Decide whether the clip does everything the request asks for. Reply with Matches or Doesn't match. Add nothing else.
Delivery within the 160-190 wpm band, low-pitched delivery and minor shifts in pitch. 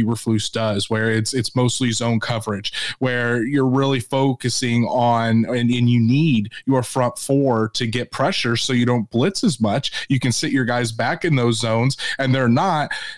Matches